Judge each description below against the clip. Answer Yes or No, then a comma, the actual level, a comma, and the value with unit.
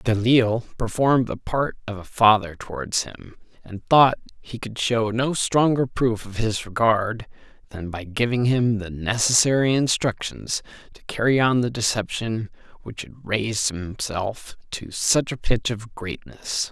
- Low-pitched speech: Yes, low, 110 Hz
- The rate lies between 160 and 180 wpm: No, average, 150 wpm